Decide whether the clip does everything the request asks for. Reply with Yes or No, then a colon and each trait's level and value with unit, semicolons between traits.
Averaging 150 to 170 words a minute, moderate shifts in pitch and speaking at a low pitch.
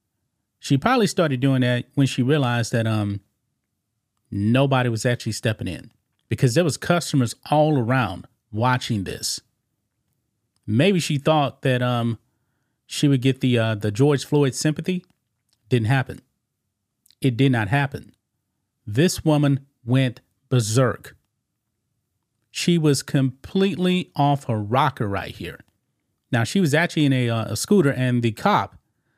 No: average, 140 wpm; average, 3.9 semitones; low, 125 Hz